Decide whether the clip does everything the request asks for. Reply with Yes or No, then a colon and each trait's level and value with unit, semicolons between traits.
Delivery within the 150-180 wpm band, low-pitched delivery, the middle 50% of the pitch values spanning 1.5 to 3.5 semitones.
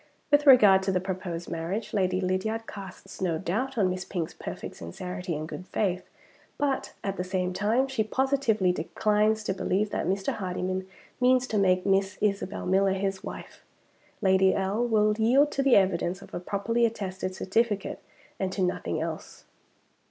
No: average, 165 wpm; high, 195 Hz; average, 2.9 semitones